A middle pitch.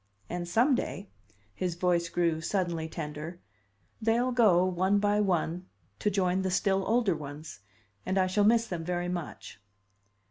Yes: medium, 180 Hz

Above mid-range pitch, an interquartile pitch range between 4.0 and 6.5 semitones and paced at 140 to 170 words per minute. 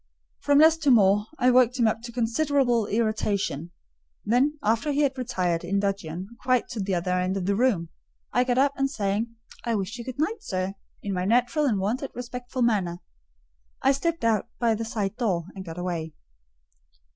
No: high, 225 Hz; average, 4.6 semitones; average, 190 wpm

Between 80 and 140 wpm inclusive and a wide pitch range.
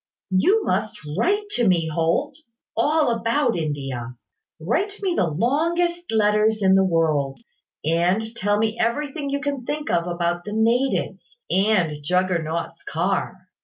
Yes: slow, 135 wpm; wide, 8.1 semitones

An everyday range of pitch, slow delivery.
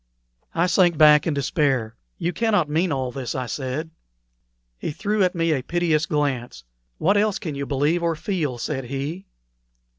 No: average, 4.4 semitones; average, 170 wpm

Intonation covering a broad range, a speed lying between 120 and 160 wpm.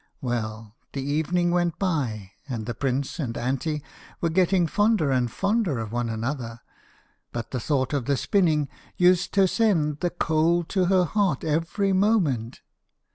Yes: wide, 6.5 semitones; average, 155 wpm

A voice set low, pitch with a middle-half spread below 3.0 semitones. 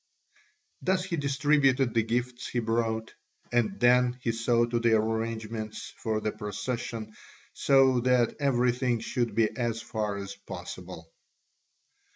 Yes: low, 115 Hz; narrow, 2.4 semitones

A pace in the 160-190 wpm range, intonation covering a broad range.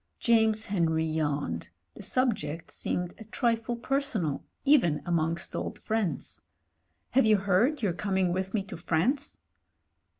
No: slow, 135 wpm; wide, 5.9 semitones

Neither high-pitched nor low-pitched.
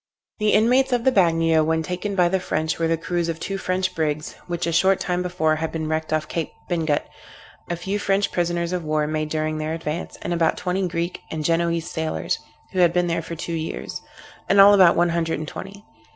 Yes: medium, 170 Hz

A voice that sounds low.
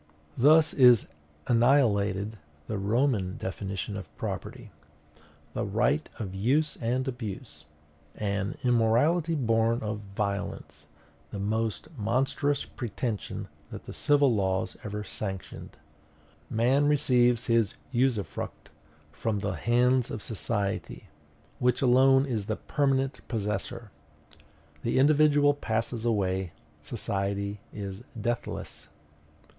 Yes: low, 115 Hz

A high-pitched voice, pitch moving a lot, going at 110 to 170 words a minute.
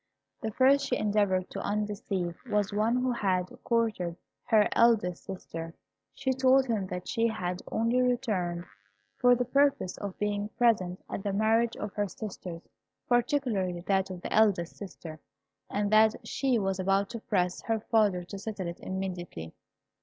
No: high, 205 Hz; average, 4.0 semitones; average, 160 wpm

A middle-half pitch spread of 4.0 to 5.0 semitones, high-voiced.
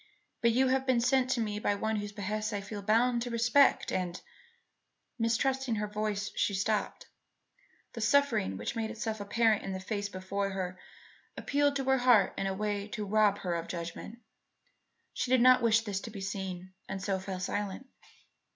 No: average, 3.3 semitones; high, 210 Hz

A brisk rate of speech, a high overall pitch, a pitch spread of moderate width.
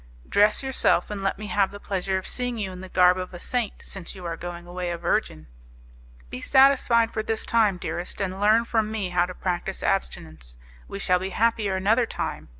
Yes: fast, 210 wpm; high, 195 Hz; average, 3.4 semitones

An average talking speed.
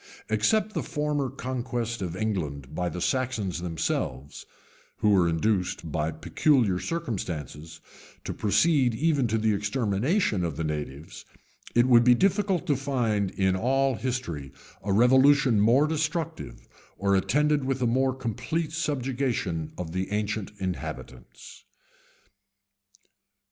No: slow, 125 wpm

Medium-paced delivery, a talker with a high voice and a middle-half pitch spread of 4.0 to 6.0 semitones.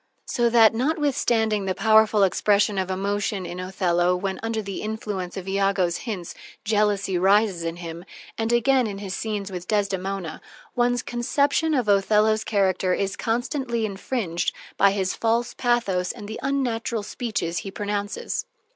No: average, 150 wpm; high, 205 Hz; average, 3.1 semitones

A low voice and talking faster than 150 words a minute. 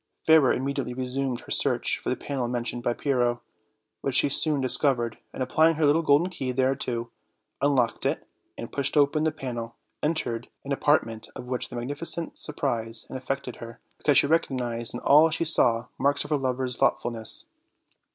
Yes: low, 130 Hz; average, 180 wpm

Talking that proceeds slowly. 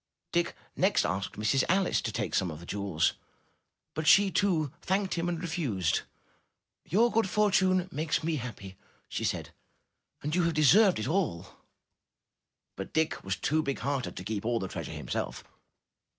No: average, 170 wpm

